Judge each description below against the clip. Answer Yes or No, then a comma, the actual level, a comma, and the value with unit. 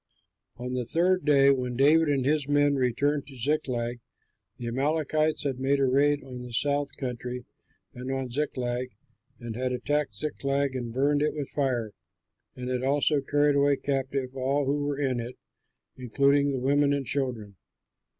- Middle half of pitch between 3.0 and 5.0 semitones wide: No, narrow, 2.4 semitones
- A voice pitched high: No, low, 135 Hz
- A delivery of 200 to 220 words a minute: No, average, 165 wpm